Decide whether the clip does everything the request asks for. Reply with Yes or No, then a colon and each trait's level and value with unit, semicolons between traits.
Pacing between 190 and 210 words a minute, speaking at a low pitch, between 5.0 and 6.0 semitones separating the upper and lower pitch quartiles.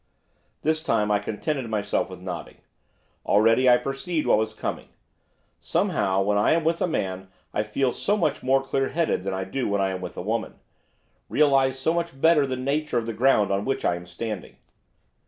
Yes: average, 195 wpm; low, 120 Hz; wide, 5.5 semitones